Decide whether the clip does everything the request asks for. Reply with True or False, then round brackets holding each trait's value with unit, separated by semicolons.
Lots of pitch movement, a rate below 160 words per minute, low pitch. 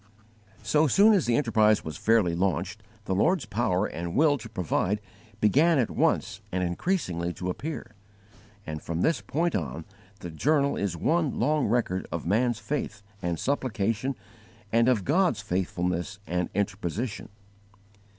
True (7.8 semitones; 145 wpm; 105 Hz)